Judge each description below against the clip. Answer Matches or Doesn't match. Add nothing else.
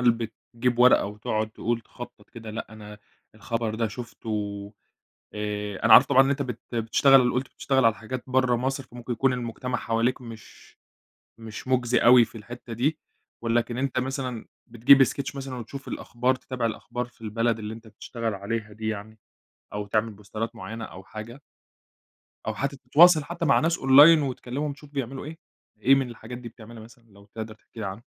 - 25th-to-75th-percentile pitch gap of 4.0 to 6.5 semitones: Doesn't match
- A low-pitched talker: Matches